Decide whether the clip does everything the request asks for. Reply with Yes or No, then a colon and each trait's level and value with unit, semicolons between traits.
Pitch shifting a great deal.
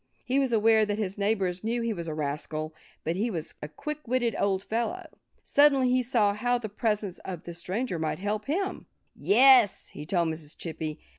Yes: wide, 6.0 semitones